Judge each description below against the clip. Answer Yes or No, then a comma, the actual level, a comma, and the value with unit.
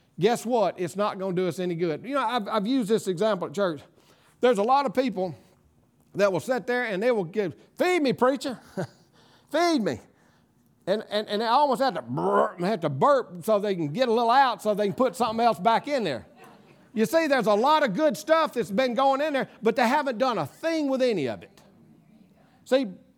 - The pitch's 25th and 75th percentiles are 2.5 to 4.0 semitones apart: No, average, 4.8 semitones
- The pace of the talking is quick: Yes, fast, 225 wpm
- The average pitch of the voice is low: No, high, 230 Hz